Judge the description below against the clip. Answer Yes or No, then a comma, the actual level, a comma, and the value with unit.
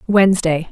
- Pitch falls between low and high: Yes, medium, 180 Hz